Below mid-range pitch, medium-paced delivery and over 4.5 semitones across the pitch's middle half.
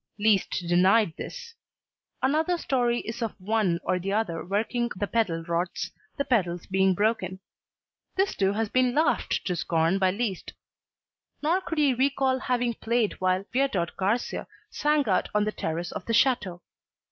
No: high, 215 Hz; average, 160 wpm; average, 5.3 semitones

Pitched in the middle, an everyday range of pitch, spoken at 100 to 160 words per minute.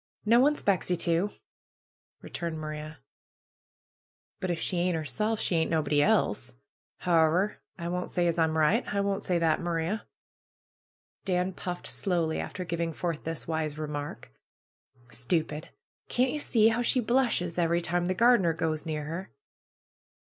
Yes: medium, 170 Hz; average, 3.0 semitones; average, 155 wpm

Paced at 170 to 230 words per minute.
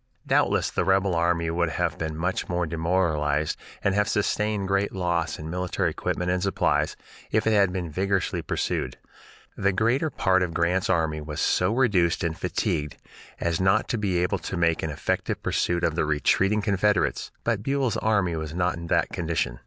Yes: average, 180 wpm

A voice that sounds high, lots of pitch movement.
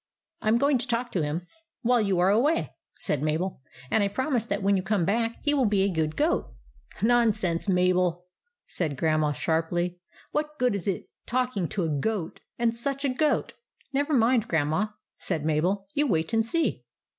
Yes: high, 200 Hz; wide, 6.0 semitones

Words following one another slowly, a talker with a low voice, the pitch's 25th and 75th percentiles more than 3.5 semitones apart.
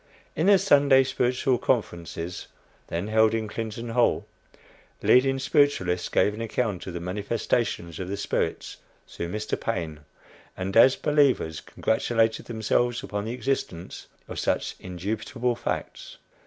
Yes: slow, 130 wpm; low, 110 Hz; average, 5.3 semitones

